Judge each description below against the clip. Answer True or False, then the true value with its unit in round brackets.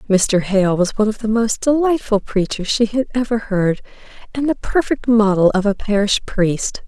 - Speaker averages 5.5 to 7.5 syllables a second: False (4.8 syllables/s)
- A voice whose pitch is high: True (215 Hz)